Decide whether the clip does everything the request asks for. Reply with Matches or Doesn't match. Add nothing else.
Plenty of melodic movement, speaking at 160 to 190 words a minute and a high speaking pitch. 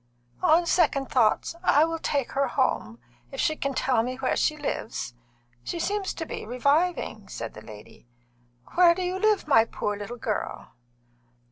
Matches